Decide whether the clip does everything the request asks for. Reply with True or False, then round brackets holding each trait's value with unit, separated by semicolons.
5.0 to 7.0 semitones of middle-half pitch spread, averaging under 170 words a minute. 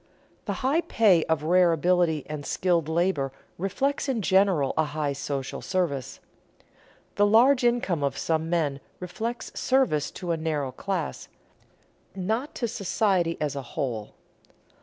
True (5.5 semitones; 140 wpm)